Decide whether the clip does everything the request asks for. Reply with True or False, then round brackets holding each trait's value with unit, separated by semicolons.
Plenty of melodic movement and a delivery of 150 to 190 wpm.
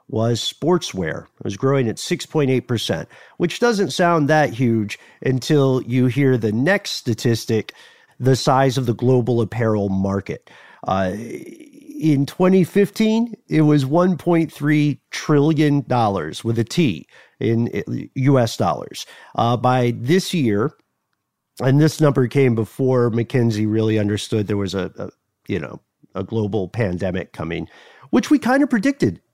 False (5.9 semitones; 135 wpm)